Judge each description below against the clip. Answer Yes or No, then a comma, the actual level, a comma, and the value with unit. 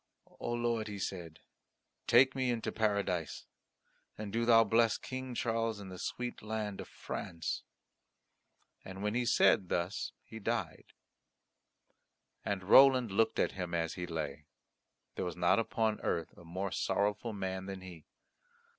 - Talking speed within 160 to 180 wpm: No, average, 150 wpm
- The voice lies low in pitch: Yes, low, 105 Hz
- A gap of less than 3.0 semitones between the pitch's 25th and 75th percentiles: No, average, 4.0 semitones